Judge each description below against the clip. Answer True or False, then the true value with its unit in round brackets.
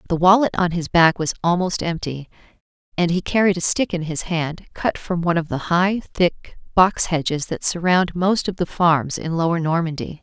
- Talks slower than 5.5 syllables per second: True (4.9 syllables/s)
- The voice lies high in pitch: False (170 Hz)